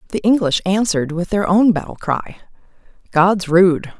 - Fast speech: No, average, 150 wpm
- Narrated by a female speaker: Yes, female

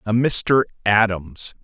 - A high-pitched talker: No, low, 110 Hz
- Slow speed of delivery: Yes, slow, 110 wpm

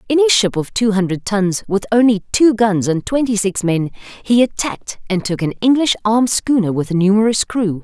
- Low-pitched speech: No, high, 210 Hz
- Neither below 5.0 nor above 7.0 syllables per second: Yes, 5.3 syllables/s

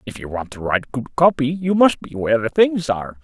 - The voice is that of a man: Yes, male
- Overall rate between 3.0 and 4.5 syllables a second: No, 5.8 syllables/s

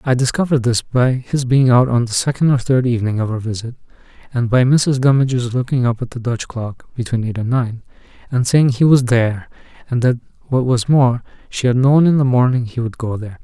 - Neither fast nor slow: No, fast, 225 wpm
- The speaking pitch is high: No, low, 125 Hz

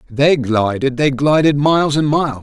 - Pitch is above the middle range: No, medium, 140 Hz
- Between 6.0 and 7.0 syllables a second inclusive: No, 4.9 syllables/s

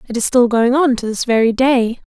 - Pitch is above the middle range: Yes, high, 240 Hz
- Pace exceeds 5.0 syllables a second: Yes, 5.3 syllables/s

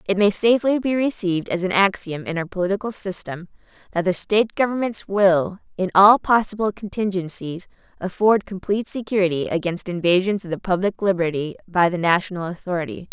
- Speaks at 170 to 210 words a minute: No, average, 155 wpm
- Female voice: Yes, female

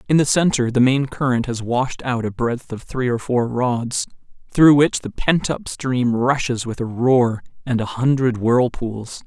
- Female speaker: No, male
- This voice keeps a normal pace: Yes, average, 195 wpm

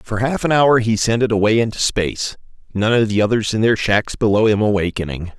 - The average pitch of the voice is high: No, low, 110 Hz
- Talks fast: Yes, fast, 225 wpm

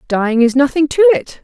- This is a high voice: Yes, very high, 285 Hz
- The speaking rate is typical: No, fast, 210 wpm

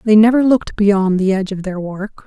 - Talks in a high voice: Yes, high, 205 Hz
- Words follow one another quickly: Yes, fast, 240 wpm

